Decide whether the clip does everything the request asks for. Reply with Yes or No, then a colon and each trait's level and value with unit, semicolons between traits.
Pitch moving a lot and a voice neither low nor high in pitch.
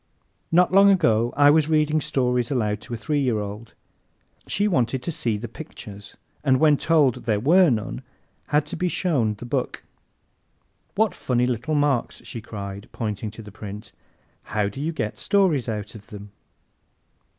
No: wide, 6.1 semitones; low, 125 Hz